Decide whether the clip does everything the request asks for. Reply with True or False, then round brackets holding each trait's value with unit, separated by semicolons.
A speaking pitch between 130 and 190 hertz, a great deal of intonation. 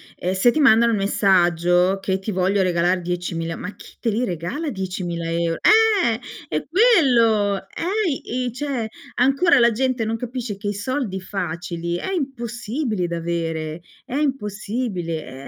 False (205 Hz; 6.2 semitones)